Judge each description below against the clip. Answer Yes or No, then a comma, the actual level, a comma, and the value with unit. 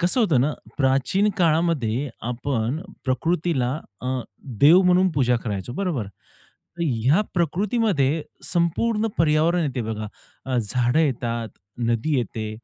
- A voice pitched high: No, medium, 140 Hz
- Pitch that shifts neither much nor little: No, wide, 5.9 semitones